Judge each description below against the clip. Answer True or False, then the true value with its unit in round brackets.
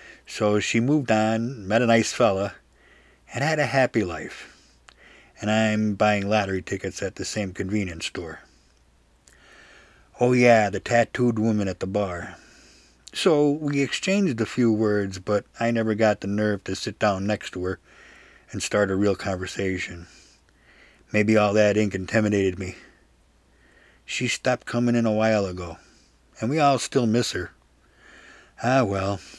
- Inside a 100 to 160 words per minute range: True (155 wpm)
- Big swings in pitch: False (3.2 semitones)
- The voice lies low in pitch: True (105 Hz)